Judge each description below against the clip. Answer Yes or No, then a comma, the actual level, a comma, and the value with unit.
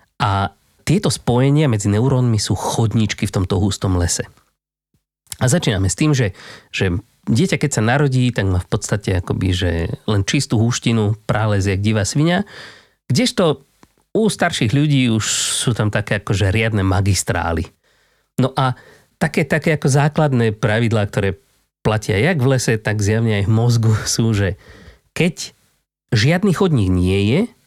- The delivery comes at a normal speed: Yes, average, 150 wpm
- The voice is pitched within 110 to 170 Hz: Yes, low, 115 Hz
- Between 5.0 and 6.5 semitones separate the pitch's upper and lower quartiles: Yes, average, 5.3 semitones